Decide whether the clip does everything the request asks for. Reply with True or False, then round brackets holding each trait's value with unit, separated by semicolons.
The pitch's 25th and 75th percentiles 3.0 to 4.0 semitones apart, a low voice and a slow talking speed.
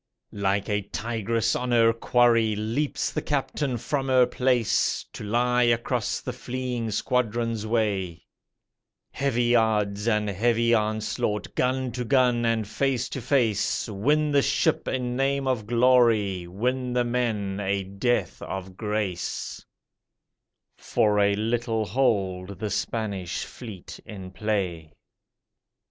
True (3.3 semitones; 115 Hz; 125 wpm)